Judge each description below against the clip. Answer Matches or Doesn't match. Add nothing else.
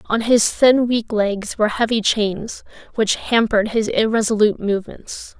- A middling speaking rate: Matches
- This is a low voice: Doesn't match